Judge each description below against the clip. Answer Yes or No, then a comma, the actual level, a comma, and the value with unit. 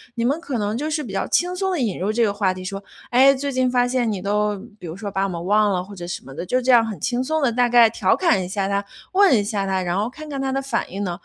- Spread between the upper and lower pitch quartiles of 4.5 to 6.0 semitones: Yes, average, 4.8 semitones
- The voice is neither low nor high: No, high, 220 Hz